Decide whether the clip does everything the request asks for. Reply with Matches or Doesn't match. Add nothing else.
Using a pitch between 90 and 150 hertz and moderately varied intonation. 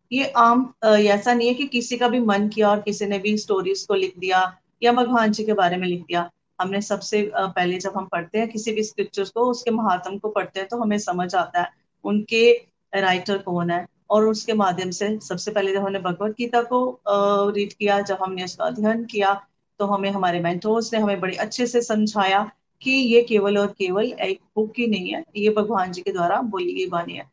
Doesn't match